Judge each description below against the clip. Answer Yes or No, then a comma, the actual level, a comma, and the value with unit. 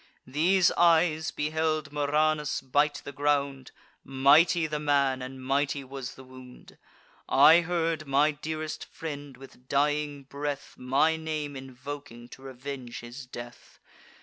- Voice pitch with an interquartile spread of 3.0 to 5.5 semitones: No, narrow, 2.6 semitones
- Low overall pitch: No, medium, 145 Hz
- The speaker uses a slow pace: Yes, slow, 125 wpm